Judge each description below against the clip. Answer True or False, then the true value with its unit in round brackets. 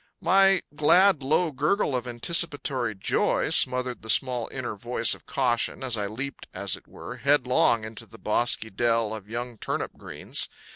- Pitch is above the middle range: False (125 Hz)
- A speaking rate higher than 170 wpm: False (160 wpm)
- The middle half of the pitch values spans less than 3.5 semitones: False (4.2 semitones)